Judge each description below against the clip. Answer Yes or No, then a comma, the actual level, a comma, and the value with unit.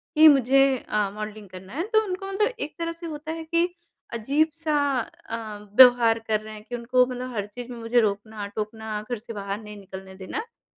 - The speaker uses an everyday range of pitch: No, wide, 6.4 semitones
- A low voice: No, high, 235 Hz